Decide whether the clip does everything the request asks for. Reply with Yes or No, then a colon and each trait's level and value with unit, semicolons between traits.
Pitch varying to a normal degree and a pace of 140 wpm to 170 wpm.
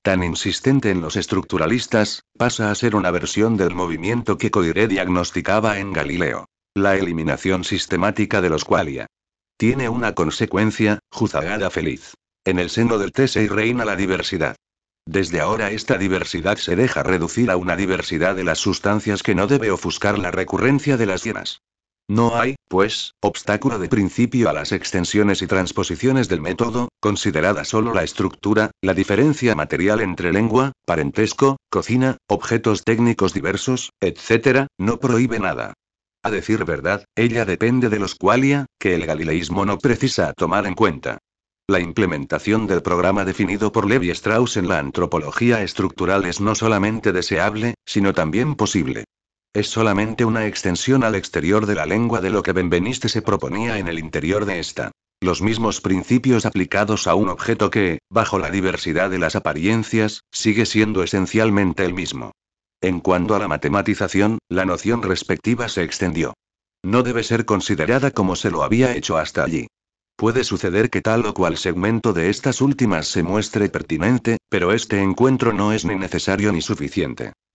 Yes: average, 3.6 semitones; average, 160 wpm